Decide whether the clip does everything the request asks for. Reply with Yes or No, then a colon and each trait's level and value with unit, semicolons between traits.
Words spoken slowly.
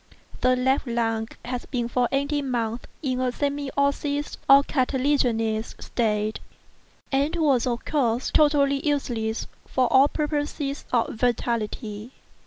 Yes: slow, 125 wpm